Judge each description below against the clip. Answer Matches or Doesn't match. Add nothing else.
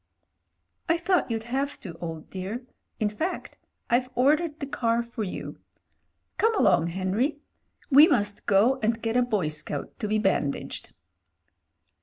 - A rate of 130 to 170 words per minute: Matches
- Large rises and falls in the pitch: Matches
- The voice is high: Matches